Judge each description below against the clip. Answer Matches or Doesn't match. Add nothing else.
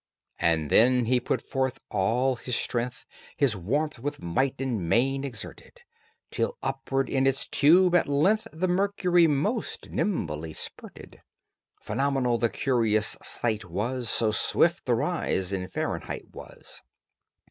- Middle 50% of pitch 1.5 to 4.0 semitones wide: Doesn't match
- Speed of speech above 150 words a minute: Doesn't match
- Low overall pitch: Matches